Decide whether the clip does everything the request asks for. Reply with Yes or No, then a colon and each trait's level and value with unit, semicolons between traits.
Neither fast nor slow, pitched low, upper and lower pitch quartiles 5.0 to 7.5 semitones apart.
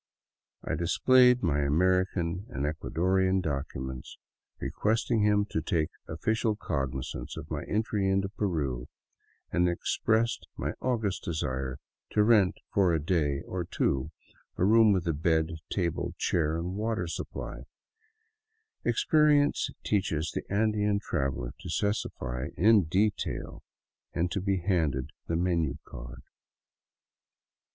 No: slow, 130 wpm; very low, 90 Hz; average, 5.3 semitones